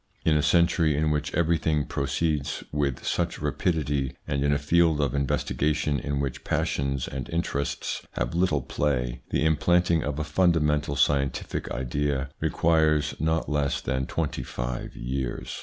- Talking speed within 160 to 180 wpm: No, average, 145 wpm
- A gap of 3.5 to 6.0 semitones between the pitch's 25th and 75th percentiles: No, narrow, 2.4 semitones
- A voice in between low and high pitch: No, very low, 75 Hz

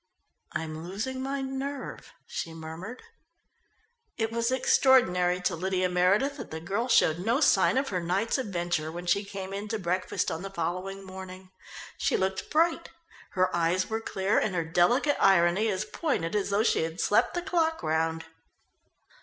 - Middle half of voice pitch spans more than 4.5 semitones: Yes, average, 5.1 semitones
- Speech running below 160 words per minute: No, average, 165 wpm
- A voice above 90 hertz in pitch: Yes, high, 190 Hz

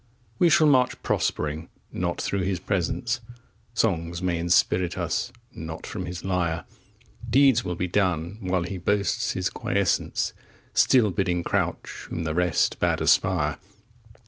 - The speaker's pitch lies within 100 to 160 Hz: No, very low, 90 Hz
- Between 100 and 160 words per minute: Yes, average, 140 wpm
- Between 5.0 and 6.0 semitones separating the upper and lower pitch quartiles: No, average, 3.2 semitones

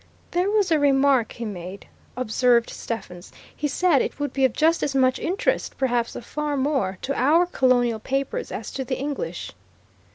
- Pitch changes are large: No, average, 3.9 semitones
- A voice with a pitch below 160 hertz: No, very high, 270 Hz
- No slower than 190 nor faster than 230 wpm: No, average, 175 wpm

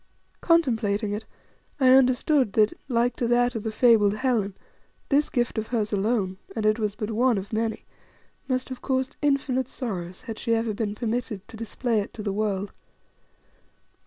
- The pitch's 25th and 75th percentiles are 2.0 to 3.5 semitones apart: Yes, average, 3.1 semitones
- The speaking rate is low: No, average, 175 wpm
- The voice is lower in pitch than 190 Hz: No, high, 225 Hz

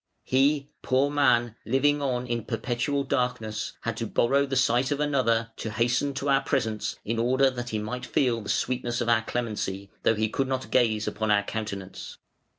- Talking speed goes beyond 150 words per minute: Yes, average, 185 wpm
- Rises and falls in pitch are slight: No, average, 3.1 semitones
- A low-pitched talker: Yes, low, 120 Hz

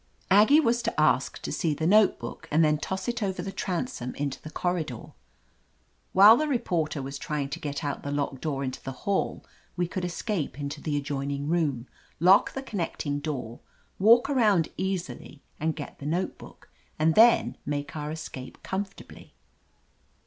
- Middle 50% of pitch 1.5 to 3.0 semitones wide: No, average, 5.3 semitones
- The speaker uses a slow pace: No, average, 165 wpm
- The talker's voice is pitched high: No, medium, 160 Hz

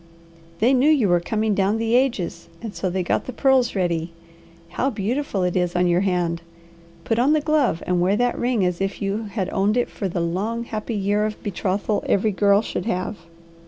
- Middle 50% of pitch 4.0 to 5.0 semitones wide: Yes, average, 4.3 semitones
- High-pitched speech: Yes, high, 205 Hz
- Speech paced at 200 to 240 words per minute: Yes, fast, 205 wpm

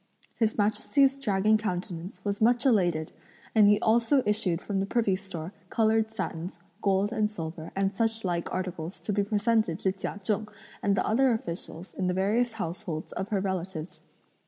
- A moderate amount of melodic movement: Yes, average, 3.3 semitones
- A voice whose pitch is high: Yes, high, 200 Hz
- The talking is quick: No, average, 170 wpm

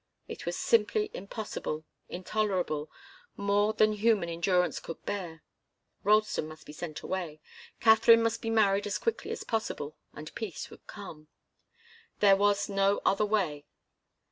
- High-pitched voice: Yes, high, 200 Hz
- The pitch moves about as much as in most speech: Yes, average, 4.2 semitones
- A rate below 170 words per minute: Yes, average, 140 wpm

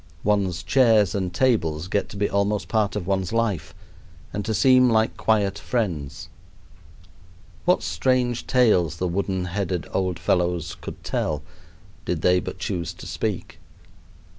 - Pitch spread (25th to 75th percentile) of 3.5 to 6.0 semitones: Yes, average, 3.8 semitones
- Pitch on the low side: Yes, low, 100 Hz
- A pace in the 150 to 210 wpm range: No, average, 140 wpm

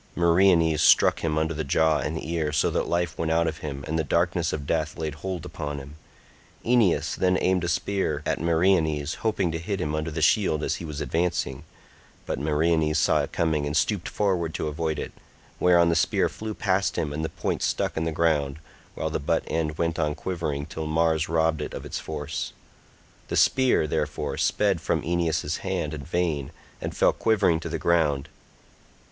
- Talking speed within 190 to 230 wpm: Yes, average, 195 wpm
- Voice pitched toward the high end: No, very low, 80 Hz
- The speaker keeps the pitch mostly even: Yes, narrow, 2.2 semitones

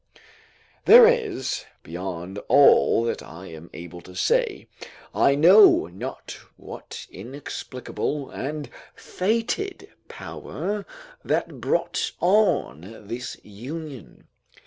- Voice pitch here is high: No, low, 135 Hz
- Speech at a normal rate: No, slow, 95 wpm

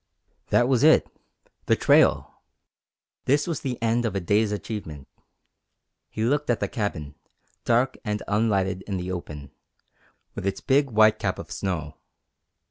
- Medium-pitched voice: No, low, 105 Hz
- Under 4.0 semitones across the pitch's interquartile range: No, average, 4.4 semitones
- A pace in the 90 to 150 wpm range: Yes, average, 145 wpm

